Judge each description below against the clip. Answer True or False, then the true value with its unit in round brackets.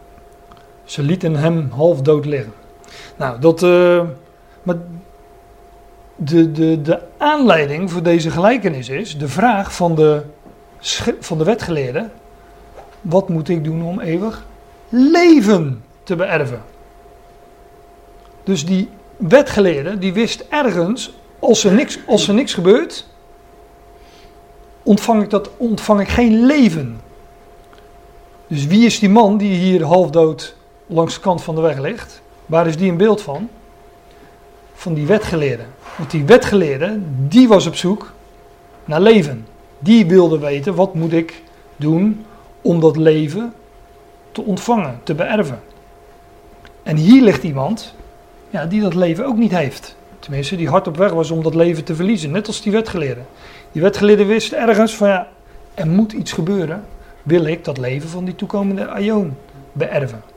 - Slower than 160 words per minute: True (145 wpm)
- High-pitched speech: False (180 Hz)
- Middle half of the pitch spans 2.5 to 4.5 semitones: False (4.9 semitones)